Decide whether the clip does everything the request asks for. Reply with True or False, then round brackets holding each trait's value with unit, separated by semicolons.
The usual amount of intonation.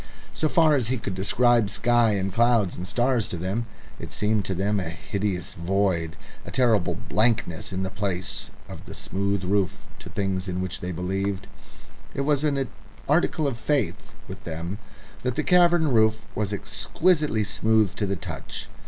True (4.2 semitones)